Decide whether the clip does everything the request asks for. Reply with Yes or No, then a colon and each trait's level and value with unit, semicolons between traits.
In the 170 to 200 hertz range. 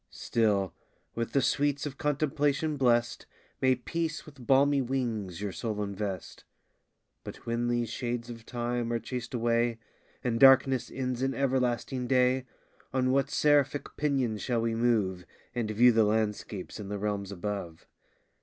No: low, 120 Hz